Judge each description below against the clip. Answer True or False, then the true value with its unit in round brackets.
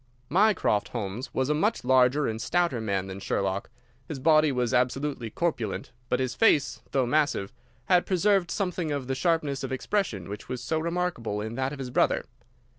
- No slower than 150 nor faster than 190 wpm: True (180 wpm)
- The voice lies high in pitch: False (135 Hz)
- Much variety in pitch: True (5.8 semitones)